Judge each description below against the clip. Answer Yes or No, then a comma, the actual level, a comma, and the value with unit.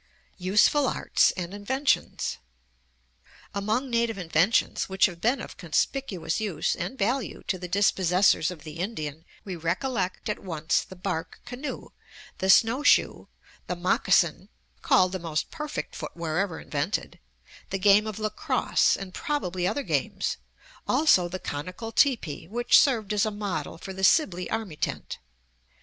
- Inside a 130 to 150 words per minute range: Yes, average, 140 wpm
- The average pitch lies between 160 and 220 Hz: Yes, high, 190 Hz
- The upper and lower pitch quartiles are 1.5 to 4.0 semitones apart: No, average, 4.4 semitones